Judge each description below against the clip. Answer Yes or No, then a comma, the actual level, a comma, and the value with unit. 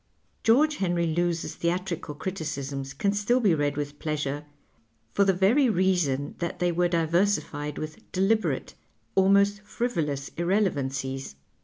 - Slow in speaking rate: Yes, slow, 125 wpm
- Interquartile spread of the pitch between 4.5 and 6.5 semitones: Yes, average, 5.2 semitones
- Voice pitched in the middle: Yes, medium, 175 Hz